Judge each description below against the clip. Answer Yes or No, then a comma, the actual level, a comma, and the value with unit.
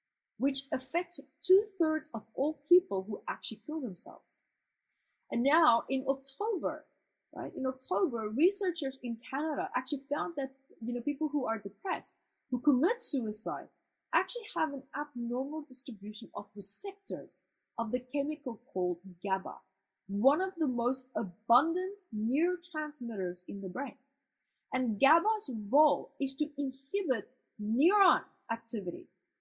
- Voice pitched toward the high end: Yes, very high, 270 Hz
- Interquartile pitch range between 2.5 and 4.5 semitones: No, average, 5.3 semitones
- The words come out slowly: Yes, slow, 125 wpm